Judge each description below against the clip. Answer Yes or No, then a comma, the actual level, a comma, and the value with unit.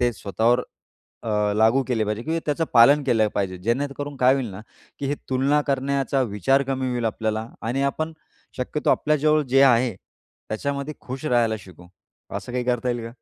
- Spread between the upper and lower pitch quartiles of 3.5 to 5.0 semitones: Yes, average, 3.8 semitones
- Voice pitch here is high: No, low, 125 Hz